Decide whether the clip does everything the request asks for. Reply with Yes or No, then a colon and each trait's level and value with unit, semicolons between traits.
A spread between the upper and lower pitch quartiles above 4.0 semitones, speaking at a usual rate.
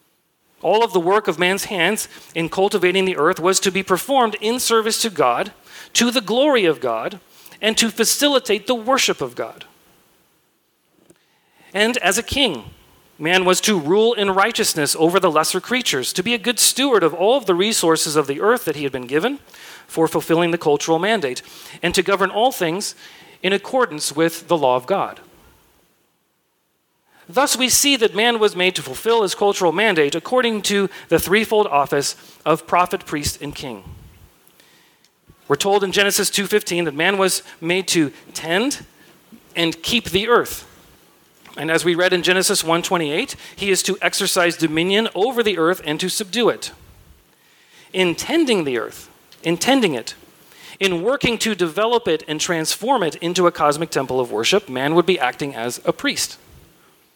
Yes: average, 4.8 semitones; average, 170 wpm